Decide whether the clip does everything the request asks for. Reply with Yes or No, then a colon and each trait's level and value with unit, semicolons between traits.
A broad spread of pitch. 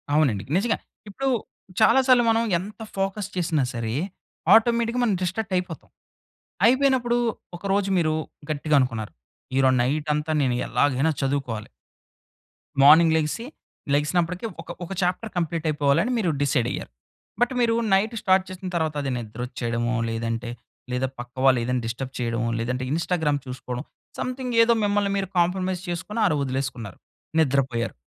Yes: wide, 7.4 semitones